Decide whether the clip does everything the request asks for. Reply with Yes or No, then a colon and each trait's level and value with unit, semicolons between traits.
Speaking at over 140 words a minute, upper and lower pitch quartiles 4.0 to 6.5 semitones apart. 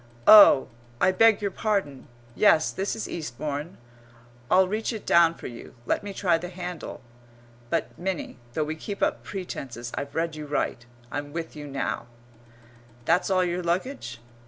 Yes: average, 160 wpm; average, 4.7 semitones